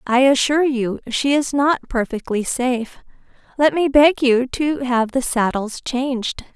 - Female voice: Yes, female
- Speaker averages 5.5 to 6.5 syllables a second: No, 4.3 syllables/s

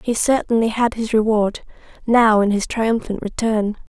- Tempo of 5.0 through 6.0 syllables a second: No, 4.6 syllables/s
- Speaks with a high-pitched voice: Yes, high, 220 Hz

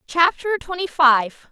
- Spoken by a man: No, female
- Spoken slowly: Yes, slow, 120 wpm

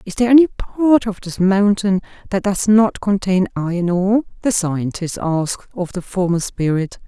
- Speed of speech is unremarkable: Yes, average, 170 wpm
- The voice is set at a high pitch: Yes, high, 195 Hz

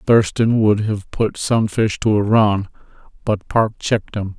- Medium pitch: No, low, 105 Hz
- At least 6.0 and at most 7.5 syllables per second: No, 4.1 syllables/s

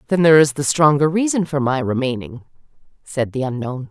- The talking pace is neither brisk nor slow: Yes, average, 185 wpm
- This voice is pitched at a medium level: Yes, medium, 145 Hz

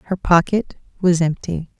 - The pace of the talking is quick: No, slow, 135 wpm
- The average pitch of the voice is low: No, medium, 175 Hz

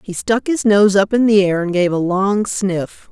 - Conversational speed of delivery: No, fast, 250 wpm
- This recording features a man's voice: No, female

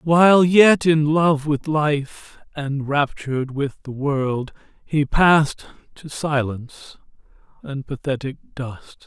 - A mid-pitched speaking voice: Yes, medium, 145 Hz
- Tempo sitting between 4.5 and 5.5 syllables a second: No, 3.5 syllables/s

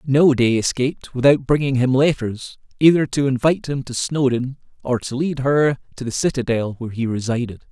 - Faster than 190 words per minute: No, average, 180 wpm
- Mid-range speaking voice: No, low, 130 Hz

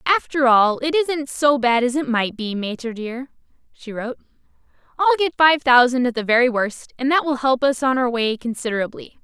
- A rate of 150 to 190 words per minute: No, average, 200 wpm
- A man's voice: No, female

